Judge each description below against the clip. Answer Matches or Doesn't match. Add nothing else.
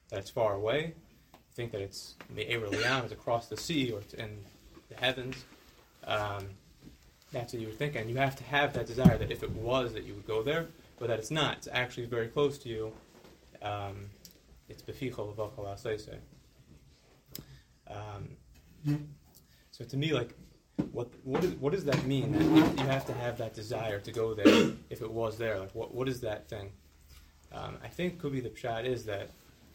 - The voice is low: Matches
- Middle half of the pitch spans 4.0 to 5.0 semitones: Matches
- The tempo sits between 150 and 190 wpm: Matches